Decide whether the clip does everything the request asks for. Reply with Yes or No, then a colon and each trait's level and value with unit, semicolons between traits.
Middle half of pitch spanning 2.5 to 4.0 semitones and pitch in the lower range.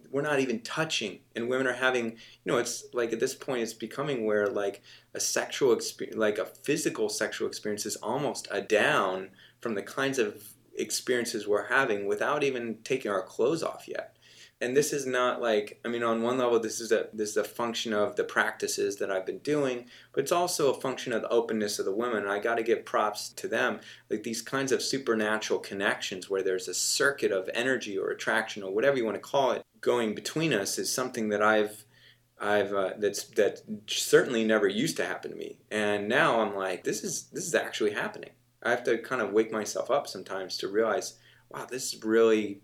No: average, 4.4 semitones; low, 120 Hz